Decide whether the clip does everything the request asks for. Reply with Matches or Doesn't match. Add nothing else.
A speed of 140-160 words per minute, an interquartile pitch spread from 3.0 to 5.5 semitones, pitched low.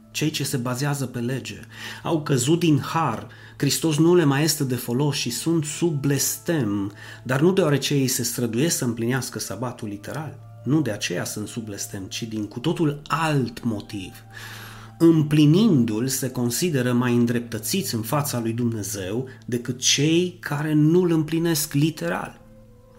Matches